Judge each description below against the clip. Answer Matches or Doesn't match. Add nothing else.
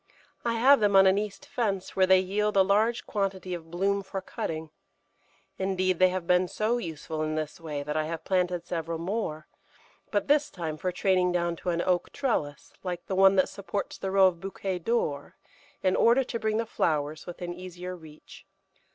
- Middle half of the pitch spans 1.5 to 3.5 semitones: Matches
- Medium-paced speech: Matches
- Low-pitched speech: Doesn't match